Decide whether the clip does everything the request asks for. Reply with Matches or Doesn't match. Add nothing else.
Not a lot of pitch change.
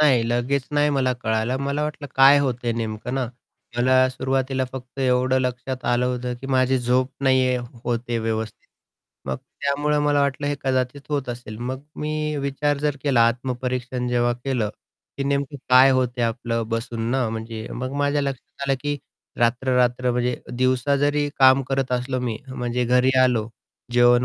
Matches